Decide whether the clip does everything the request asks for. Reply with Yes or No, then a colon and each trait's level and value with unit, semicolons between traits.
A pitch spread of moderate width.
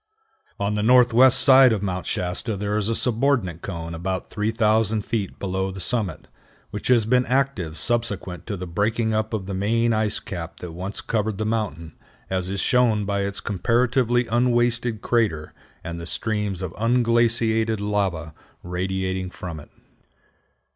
Yes: average, 3.7 semitones